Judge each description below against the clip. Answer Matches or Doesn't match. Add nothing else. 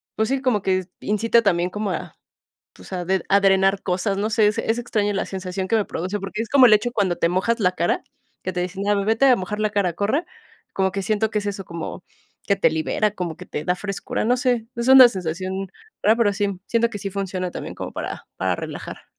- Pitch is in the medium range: Doesn't match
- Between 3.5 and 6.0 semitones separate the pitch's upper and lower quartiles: Doesn't match